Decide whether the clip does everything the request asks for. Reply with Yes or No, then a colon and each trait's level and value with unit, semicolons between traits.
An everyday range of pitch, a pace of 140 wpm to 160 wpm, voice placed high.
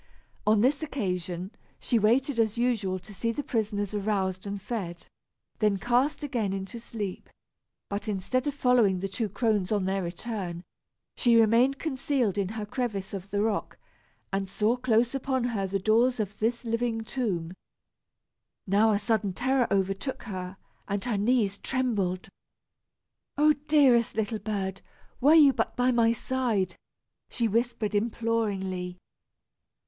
Yes: average, 3.8 semitones; average, 145 wpm; high, 215 Hz